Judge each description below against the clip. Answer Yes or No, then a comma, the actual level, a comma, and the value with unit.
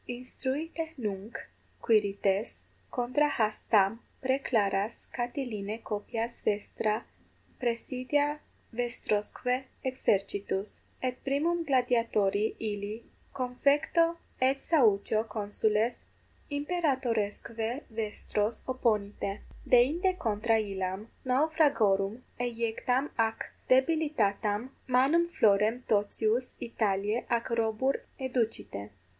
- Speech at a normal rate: No, slow, 80 wpm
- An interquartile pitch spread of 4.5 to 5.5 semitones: No, average, 3.8 semitones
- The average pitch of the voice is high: Yes, high, 230 Hz